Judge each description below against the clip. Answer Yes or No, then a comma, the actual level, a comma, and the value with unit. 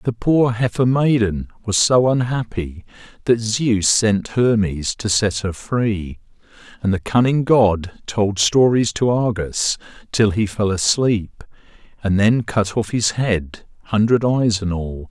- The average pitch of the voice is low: Yes, low, 110 Hz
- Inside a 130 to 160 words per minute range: Yes, average, 145 wpm